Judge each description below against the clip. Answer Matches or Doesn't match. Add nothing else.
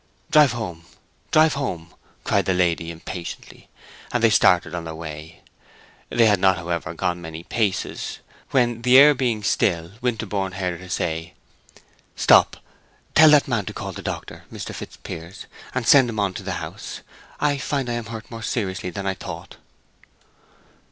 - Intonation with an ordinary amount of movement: Doesn't match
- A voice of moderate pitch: Doesn't match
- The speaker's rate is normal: Matches